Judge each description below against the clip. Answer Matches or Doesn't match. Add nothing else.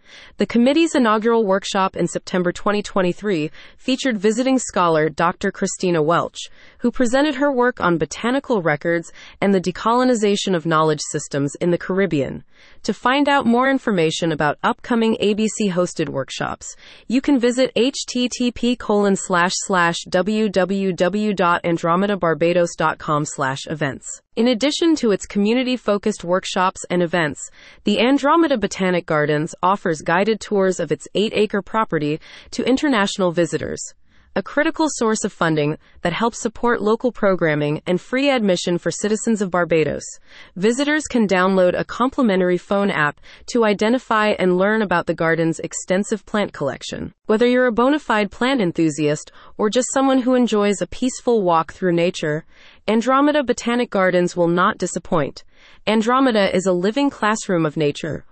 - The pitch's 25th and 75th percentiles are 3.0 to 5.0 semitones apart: Doesn't match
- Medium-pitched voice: Doesn't match